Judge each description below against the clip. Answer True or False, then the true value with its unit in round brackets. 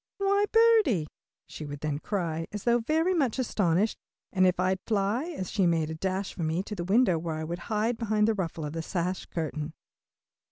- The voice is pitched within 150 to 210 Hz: True (190 Hz)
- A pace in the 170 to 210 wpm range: True (205 wpm)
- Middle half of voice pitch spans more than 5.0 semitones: True (5.5 semitones)